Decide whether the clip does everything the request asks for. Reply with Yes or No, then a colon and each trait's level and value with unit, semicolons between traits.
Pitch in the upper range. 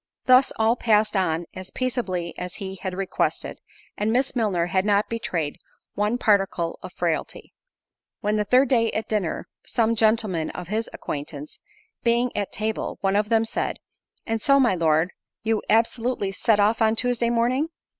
Yes: high, 215 Hz